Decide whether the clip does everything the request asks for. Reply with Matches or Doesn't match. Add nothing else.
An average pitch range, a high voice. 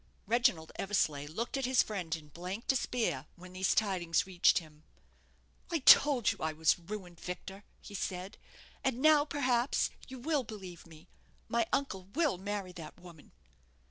Doesn't match